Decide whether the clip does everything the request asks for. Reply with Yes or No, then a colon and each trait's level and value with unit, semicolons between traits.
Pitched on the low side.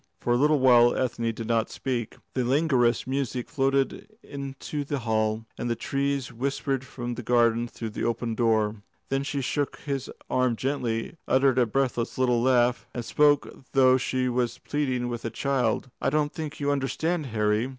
Yes: low, 125 Hz